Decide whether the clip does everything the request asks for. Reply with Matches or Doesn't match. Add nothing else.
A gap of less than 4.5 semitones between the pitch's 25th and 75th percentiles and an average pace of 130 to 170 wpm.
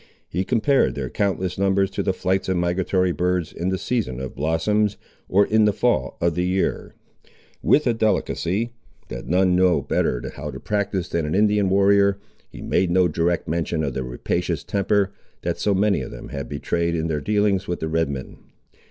Doesn't match